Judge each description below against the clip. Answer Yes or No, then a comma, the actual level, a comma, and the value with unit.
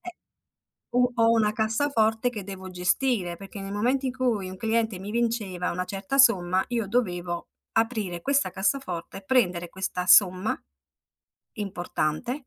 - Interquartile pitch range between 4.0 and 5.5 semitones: Yes, average, 4.5 semitones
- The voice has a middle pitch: No, high, 210 Hz